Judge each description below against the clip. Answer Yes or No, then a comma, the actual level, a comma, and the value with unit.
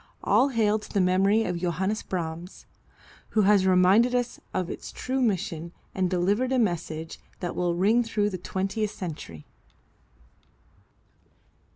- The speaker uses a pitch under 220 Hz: Yes, high, 190 Hz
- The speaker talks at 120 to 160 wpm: Yes, average, 140 wpm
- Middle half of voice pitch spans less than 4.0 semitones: Yes, average, 3.6 semitones